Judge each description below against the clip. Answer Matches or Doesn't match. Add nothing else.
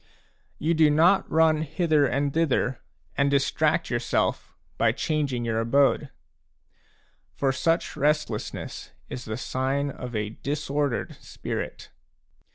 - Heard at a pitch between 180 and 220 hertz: Doesn't match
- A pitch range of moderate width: Matches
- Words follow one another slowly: Matches